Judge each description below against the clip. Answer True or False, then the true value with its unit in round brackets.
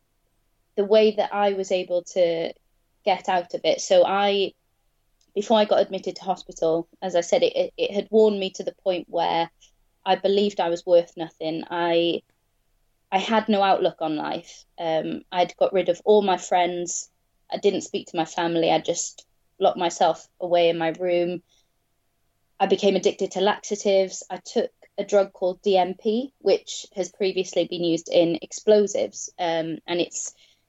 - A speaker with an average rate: True (170 wpm)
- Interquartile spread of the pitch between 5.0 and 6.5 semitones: False (3.2 semitones)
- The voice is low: False (180 Hz)